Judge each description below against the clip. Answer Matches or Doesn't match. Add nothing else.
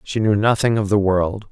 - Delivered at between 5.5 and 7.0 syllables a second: Doesn't match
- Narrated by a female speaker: Doesn't match